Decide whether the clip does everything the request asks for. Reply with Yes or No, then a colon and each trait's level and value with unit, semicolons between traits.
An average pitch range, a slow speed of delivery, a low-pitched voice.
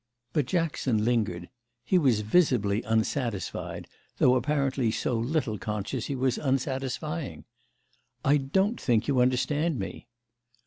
Yes: average, 4.5 semitones; slow, 120 wpm; low, 130 Hz